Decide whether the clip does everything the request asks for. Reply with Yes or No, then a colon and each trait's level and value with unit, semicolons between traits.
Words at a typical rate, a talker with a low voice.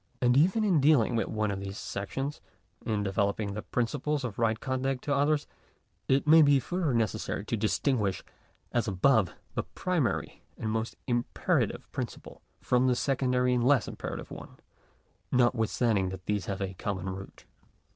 Yes: average, 160 wpm; low, 120 Hz